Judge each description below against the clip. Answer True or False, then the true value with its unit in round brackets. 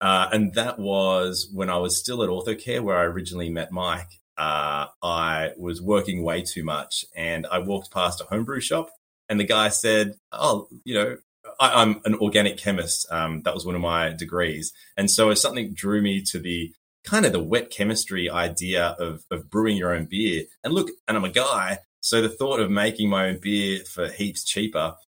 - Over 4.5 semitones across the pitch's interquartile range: False (3.1 semitones)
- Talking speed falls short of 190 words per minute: False (200 wpm)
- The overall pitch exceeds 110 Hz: False (90 Hz)